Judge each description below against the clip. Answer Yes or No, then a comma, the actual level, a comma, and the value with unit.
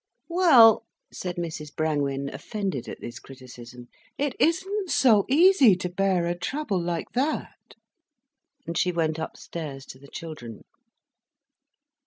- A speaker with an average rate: No, slow, 125 wpm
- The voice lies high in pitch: No, medium, 175 Hz